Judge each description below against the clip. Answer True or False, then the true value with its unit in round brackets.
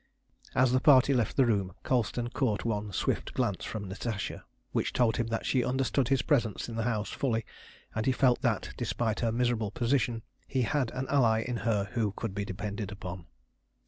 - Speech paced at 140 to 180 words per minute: False (190 wpm)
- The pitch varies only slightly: False (3.1 semitones)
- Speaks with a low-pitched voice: True (115 Hz)